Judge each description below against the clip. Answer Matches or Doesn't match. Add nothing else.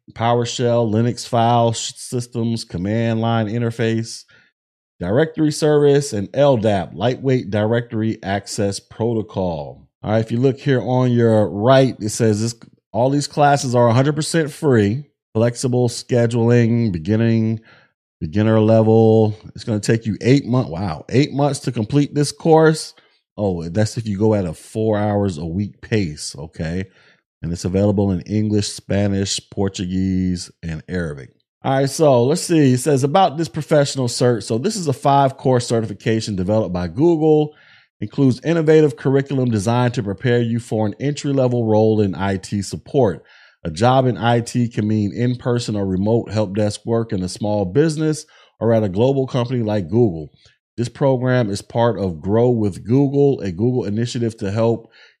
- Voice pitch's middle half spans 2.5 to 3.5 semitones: Doesn't match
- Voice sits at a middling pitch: Doesn't match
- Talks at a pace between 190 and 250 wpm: Doesn't match